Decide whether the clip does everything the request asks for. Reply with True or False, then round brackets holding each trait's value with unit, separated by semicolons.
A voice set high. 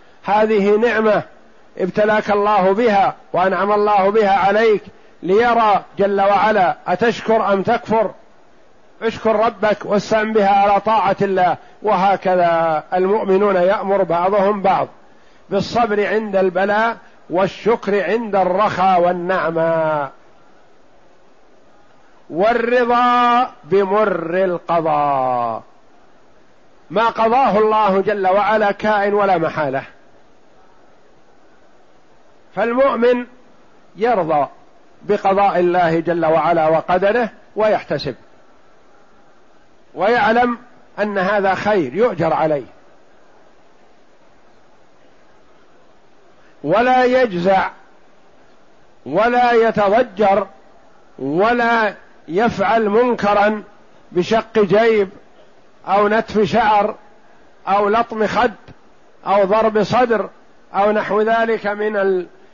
True (205 Hz)